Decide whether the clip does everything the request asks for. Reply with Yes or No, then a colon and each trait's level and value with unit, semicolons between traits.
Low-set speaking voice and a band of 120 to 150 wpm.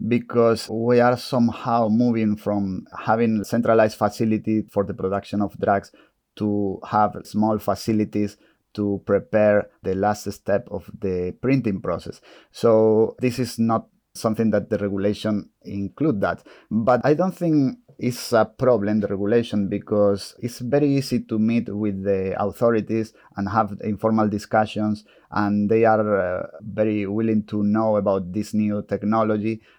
Yes: low, 105 Hz; average, 140 wpm